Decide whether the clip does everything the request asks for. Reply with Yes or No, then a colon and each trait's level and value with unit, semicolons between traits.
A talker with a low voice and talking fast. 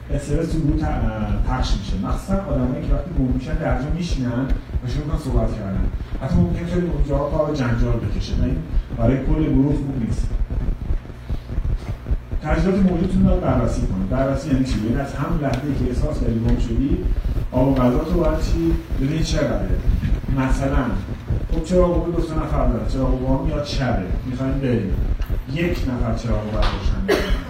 Yes: low, 130 Hz; fast, 160 wpm